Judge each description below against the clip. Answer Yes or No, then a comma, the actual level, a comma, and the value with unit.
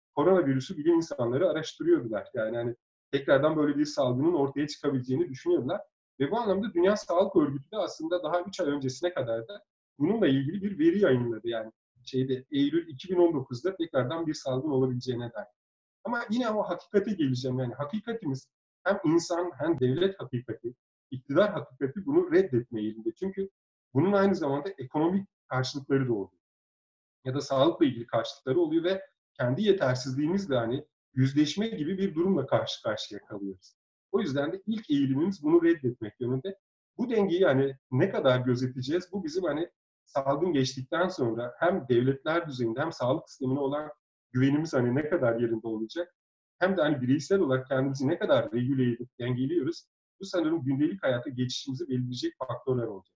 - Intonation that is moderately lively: No, wide, 6.6 semitones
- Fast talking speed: Yes, fast, 150 wpm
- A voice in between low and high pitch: Yes, medium, 145 Hz